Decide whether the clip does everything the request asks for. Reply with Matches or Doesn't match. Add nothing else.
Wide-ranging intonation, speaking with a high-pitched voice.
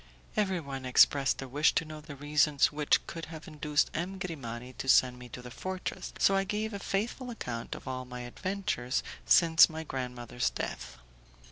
Doesn't match